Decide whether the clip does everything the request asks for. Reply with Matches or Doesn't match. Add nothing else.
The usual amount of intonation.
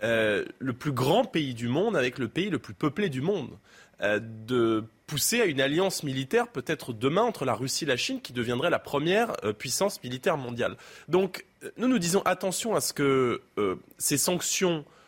Doesn't match